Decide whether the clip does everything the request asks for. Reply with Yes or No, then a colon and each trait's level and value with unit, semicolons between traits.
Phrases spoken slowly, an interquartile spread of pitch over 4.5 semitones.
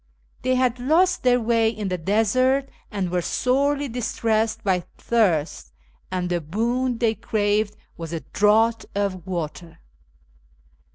Yes: slow, 130 wpm; average, 5.1 semitones